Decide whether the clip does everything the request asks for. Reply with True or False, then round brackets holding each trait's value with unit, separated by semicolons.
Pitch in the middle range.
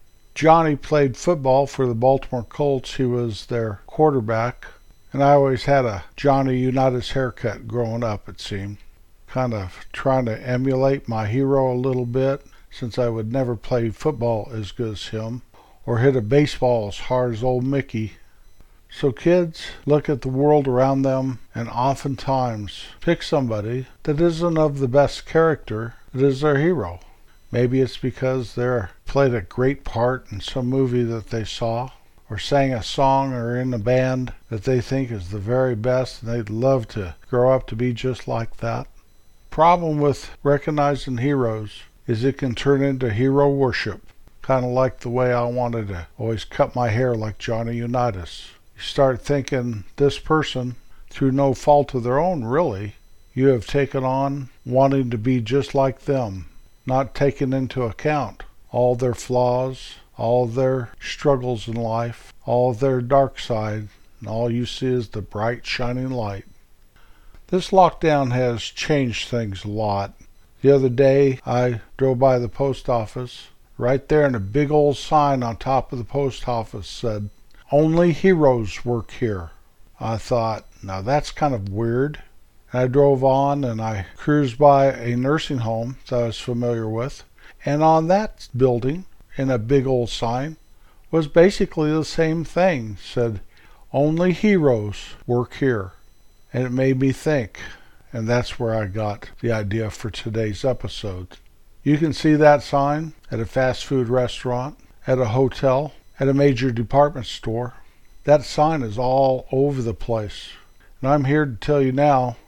False (125 Hz)